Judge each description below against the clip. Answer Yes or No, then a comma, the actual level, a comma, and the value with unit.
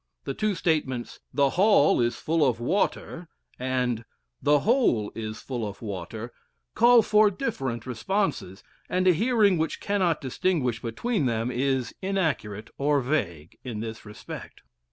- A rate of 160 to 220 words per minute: No, average, 140 wpm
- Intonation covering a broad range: Yes, wide, 8.2 semitones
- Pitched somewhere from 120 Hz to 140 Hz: Yes, low, 135 Hz